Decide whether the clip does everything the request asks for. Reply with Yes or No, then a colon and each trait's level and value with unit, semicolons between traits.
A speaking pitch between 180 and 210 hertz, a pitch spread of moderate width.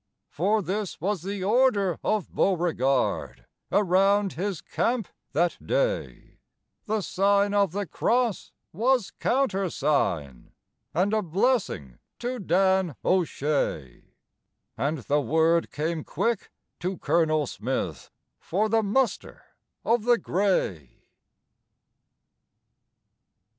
Yes: high, 190 Hz; average, 4.9 semitones